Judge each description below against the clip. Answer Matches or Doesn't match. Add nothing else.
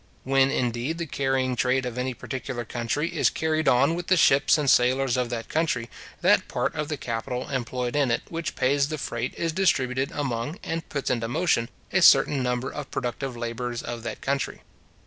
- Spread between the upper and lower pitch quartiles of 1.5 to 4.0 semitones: Matches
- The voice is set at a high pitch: Doesn't match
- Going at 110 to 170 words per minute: Doesn't match